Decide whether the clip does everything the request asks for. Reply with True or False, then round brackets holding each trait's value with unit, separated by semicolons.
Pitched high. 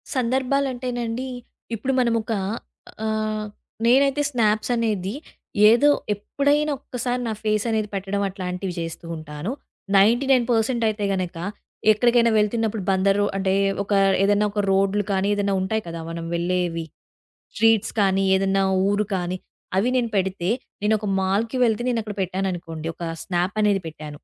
True (210 Hz)